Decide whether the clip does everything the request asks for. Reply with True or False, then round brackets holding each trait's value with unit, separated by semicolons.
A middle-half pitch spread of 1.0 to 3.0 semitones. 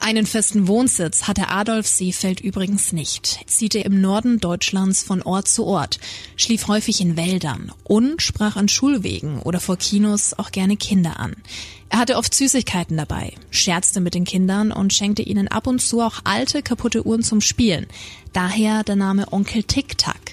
False (3.5 semitones)